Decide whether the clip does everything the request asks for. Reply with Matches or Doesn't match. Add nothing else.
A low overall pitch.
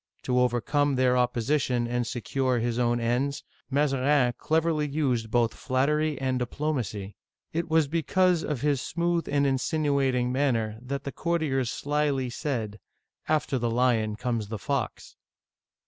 Matches